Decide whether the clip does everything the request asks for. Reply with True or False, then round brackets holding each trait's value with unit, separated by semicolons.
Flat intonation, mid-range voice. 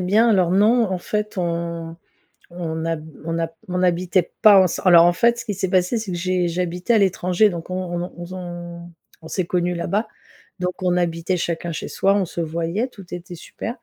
True (2.0 semitones; 180 Hz)